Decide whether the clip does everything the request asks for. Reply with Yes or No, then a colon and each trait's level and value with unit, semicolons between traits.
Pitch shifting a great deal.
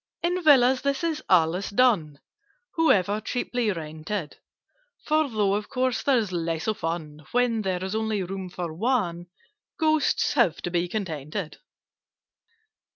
Yes: wide, 6.5 semitones